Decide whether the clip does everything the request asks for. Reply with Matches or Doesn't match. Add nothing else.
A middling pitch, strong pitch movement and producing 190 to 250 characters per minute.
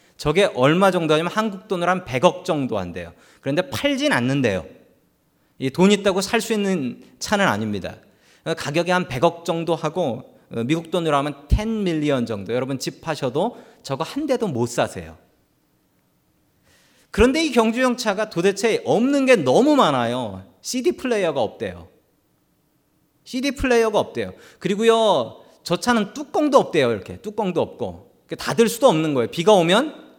Doesn't match